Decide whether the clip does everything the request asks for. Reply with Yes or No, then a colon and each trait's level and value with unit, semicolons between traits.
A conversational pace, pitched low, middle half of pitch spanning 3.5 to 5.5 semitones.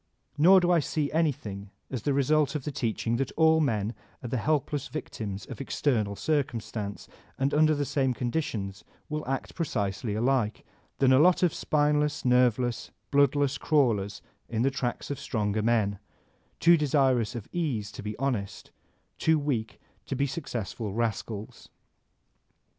Yes: average, 155 wpm; low, 130 Hz; average, 5.2 semitones